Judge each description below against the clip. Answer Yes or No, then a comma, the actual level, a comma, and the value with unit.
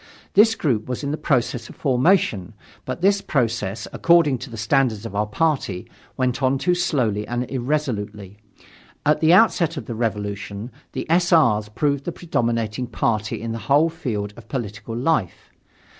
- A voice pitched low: Yes, low, 125 Hz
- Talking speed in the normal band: Yes, average, 165 wpm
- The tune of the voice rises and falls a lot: Yes, wide, 6.1 semitones